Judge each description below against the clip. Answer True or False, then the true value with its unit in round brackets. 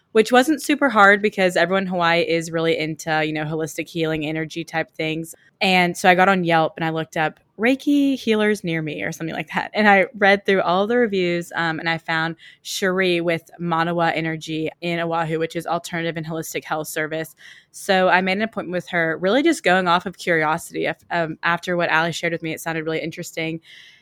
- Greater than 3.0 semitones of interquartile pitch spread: False (2.7 semitones)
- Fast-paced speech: True (210 wpm)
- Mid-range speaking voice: True (170 Hz)